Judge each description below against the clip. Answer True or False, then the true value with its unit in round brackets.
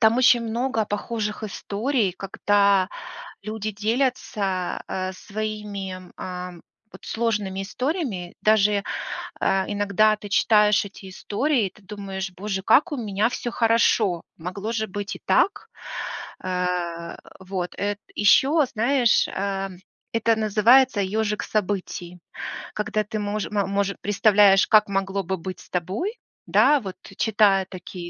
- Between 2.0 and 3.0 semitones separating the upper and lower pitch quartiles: True (2.4 semitones)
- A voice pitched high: True (205 Hz)